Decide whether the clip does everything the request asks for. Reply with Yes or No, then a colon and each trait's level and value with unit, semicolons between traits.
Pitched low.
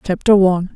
No: high, 190 Hz